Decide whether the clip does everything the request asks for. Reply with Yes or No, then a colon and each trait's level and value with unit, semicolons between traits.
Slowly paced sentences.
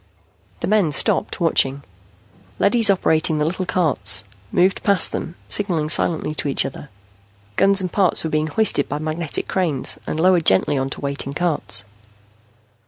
No: average, 150 wpm